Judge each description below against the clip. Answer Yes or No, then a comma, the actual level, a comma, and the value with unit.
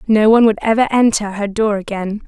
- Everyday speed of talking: No, fast, 210 wpm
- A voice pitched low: No, high, 215 Hz